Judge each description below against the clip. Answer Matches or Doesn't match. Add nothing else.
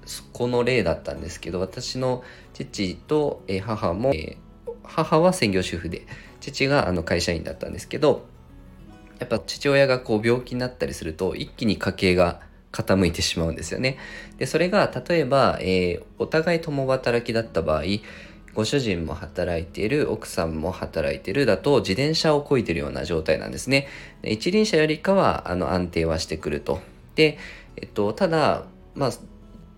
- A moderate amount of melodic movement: Doesn't match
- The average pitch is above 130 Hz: Doesn't match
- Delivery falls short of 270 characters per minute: Doesn't match